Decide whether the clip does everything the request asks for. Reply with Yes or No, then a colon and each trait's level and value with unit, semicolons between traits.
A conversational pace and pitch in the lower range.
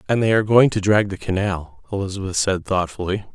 Yes: average, 195 wpm; low, 100 Hz